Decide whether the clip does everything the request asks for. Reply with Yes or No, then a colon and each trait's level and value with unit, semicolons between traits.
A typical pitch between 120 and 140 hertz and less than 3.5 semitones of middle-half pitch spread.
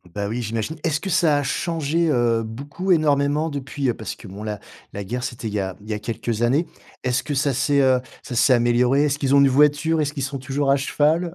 No: low, 135 Hz; average, 3.8 semitones